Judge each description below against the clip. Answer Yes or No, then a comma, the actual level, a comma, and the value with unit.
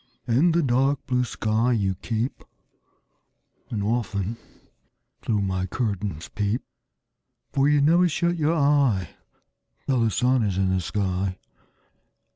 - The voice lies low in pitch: Yes, low, 115 Hz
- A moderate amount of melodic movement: No, wide, 5.8 semitones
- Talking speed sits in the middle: No, slow, 125 wpm